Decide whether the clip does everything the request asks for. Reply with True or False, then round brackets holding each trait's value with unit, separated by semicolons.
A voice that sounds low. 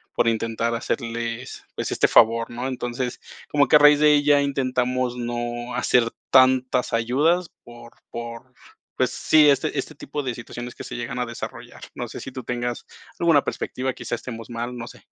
True (125 Hz)